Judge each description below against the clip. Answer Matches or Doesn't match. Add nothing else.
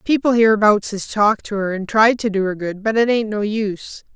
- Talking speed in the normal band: Doesn't match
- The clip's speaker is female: Matches